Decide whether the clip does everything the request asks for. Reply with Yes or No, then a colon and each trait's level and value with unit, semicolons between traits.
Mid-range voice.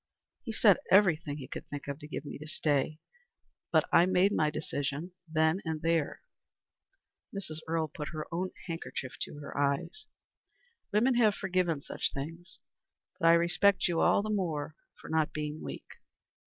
Yes: medium, 160 Hz